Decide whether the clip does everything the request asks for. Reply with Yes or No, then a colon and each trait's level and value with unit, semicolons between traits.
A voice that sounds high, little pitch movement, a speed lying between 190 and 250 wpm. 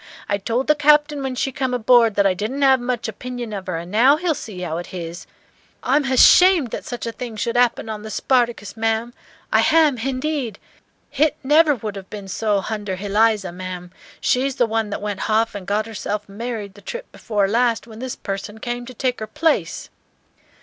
No: high, 230 Hz; average, 4.0 semitones; average, 200 wpm